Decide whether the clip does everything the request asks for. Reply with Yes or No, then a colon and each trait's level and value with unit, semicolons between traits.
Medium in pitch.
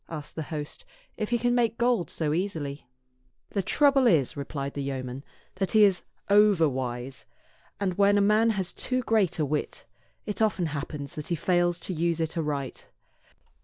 Yes: medium, 170 Hz